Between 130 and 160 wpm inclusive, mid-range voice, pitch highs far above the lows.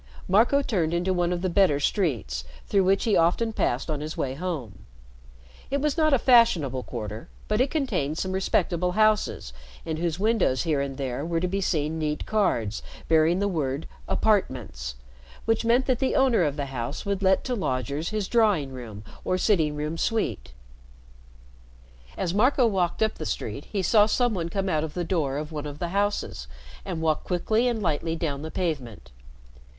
No: average, 185 wpm; medium, 170 Hz; wide, 6.3 semitones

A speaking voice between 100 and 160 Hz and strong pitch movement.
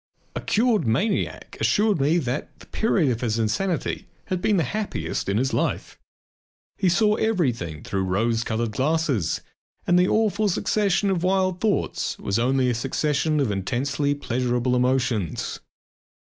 Yes: medium, 140 Hz; wide, 8.1 semitones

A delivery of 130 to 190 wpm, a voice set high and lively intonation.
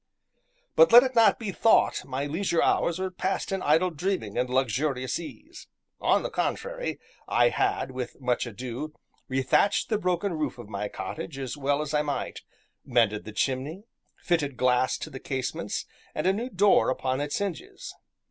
No: average, 170 wpm; medium, 150 Hz; wide, 6.8 semitones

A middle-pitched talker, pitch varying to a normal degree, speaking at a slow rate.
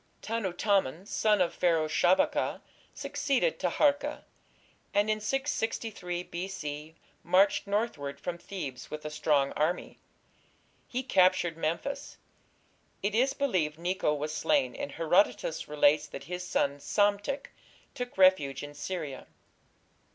No: medium, 180 Hz; wide, 5.8 semitones; slow, 120 wpm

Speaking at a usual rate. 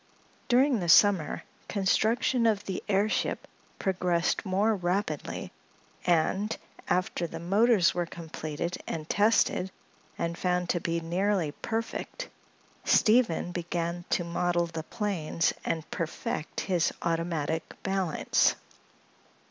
No: slow, 110 wpm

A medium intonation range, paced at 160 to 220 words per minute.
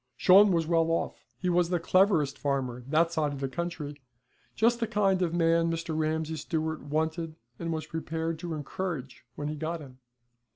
No: narrow, 2.1 semitones; average, 180 wpm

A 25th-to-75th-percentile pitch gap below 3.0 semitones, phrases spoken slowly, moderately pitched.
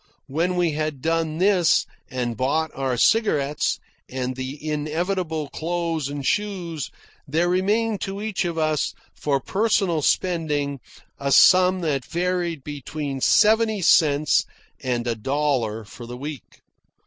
No: average, 4.5 semitones; slow, 130 wpm; medium, 155 Hz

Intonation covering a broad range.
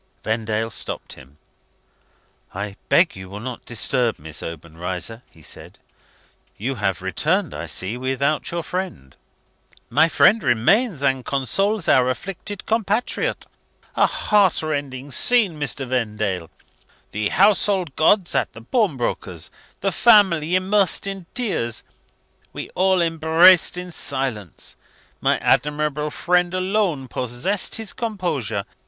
Yes: wide, 8.7 semitones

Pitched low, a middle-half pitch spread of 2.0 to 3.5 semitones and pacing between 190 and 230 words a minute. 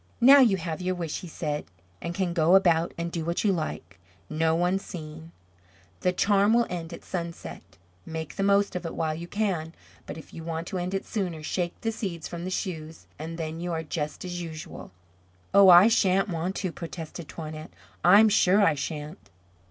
No: medium, 170 Hz; average, 2.8 semitones; average, 200 wpm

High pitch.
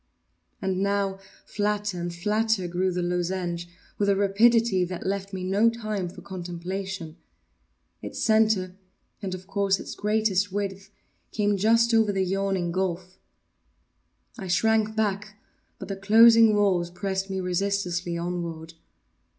Yes: high, 195 Hz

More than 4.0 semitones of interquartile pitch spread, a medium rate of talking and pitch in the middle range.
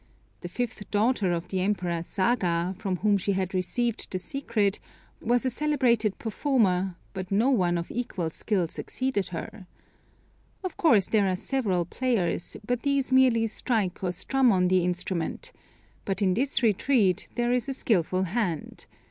No: average, 5.0 semitones; average, 155 wpm; high, 205 Hz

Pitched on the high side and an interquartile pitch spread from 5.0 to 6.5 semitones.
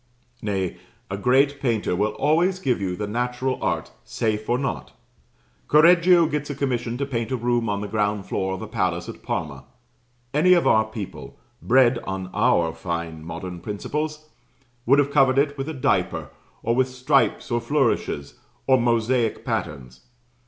No: low, 120 Hz; wide, 5.5 semitones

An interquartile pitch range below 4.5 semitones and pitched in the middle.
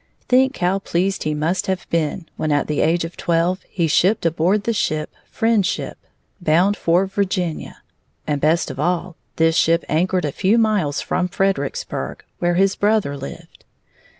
Yes: average, 3.4 semitones; medium, 175 Hz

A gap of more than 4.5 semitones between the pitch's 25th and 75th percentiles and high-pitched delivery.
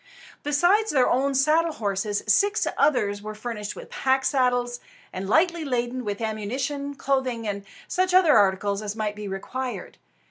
Yes: average, 5.3 semitones; high, 245 Hz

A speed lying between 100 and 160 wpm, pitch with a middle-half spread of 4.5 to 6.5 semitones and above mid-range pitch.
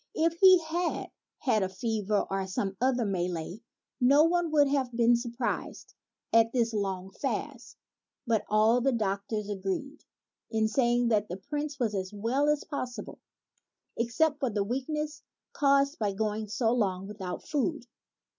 Yes: average, 155 wpm; average, 5.3 semitones; high, 235 Hz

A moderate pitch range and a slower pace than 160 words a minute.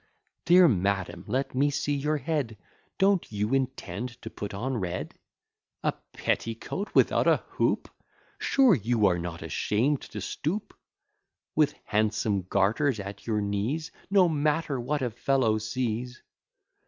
No: wide, 6.2 semitones; slow, 135 wpm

